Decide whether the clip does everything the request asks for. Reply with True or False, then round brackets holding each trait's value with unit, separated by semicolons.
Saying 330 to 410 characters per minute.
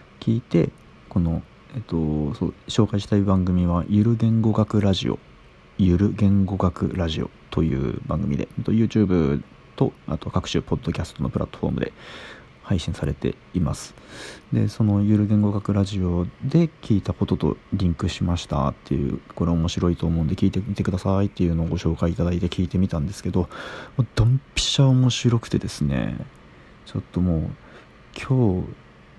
True (350 characters per minute)